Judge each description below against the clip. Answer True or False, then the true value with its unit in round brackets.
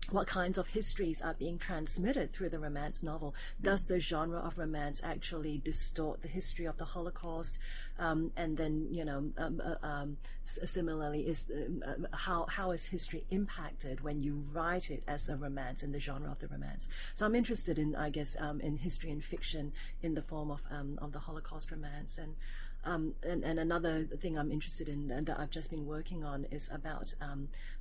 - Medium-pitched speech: True (155 Hz)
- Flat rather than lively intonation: True (2.3 semitones)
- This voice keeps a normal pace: True (195 wpm)